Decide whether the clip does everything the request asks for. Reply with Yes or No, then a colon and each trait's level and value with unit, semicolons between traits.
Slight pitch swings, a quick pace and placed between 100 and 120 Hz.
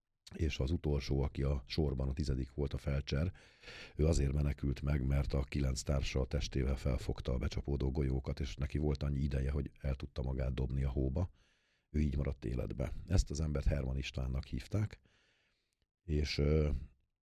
No: narrow, 2.1 semitones; fast, 165 wpm; very low, 70 Hz